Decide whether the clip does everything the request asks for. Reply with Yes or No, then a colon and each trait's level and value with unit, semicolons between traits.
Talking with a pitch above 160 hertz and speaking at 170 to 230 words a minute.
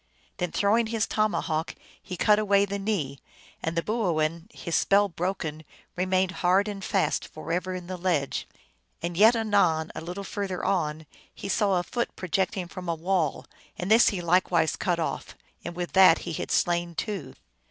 Yes: medium, 185 Hz; average, 175 wpm